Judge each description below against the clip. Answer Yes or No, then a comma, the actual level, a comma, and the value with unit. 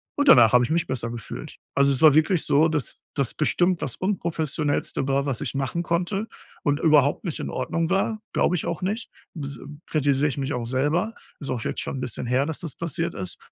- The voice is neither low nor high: Yes, medium, 150 Hz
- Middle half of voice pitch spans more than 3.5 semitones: Yes, average, 3.9 semitones